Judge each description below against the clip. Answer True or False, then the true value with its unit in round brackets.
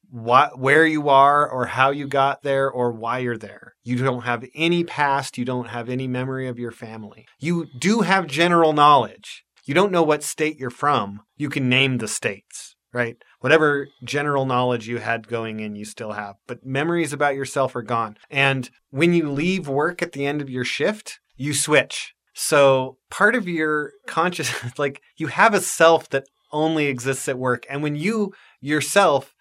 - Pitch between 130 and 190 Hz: True (140 Hz)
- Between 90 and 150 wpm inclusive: False (190 wpm)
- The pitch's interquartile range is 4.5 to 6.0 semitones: False (3.7 semitones)